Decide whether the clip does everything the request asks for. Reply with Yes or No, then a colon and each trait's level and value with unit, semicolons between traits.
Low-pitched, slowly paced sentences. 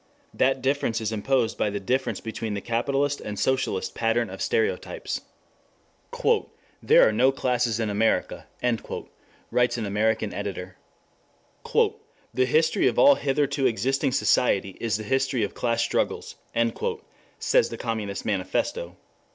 Yes: low, 115 Hz; slow, 130 wpm